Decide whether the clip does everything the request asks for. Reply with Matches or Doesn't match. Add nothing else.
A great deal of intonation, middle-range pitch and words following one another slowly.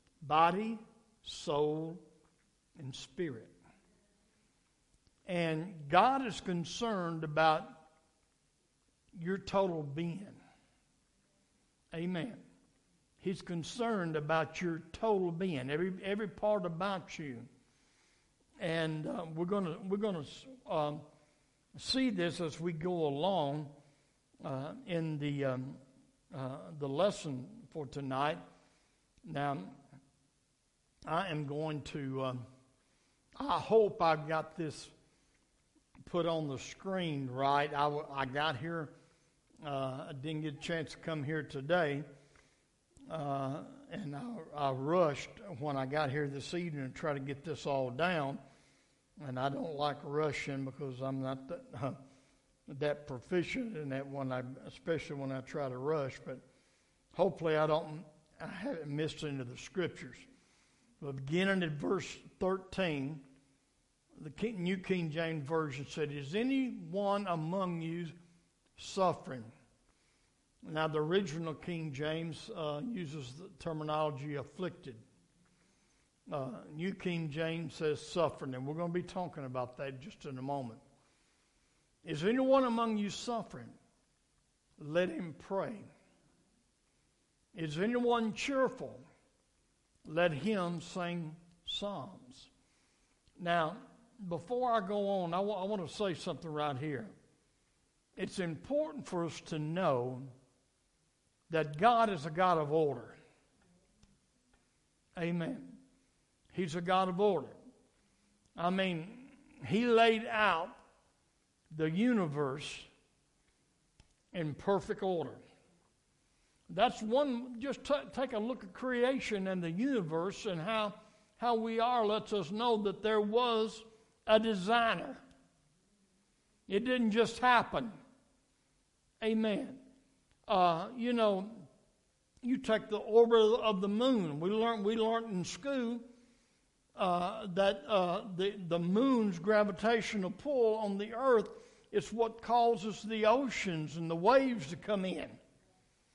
Matches